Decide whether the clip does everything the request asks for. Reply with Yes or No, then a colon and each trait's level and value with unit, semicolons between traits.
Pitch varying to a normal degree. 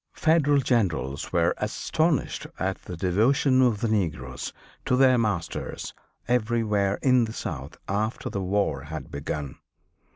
No: wide, 7.0 semitones